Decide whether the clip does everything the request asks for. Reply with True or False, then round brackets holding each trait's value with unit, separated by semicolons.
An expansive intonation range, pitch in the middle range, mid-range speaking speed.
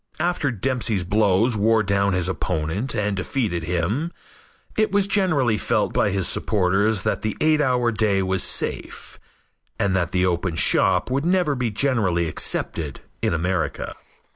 False (5.7 semitones; 105 Hz; 150 wpm)